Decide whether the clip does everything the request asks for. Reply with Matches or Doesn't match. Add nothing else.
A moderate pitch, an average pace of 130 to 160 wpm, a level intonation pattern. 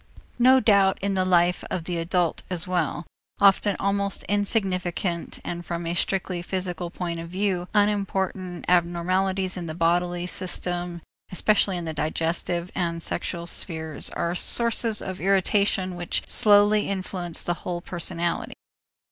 Matches